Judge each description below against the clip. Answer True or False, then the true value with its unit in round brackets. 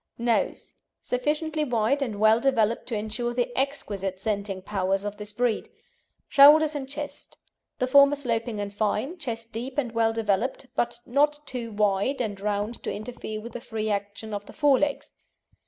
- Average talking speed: True (170 wpm)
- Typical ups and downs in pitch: True (4.3 semitones)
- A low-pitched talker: False (230 Hz)